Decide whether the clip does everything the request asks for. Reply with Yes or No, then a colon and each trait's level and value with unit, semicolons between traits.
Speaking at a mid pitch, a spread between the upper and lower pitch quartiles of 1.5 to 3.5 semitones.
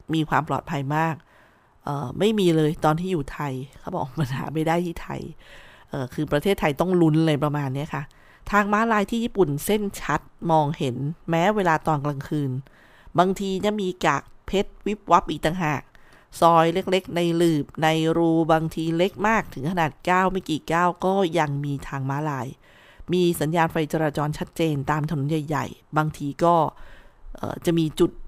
Yes: medium, 160 Hz; average, 3.1 semitones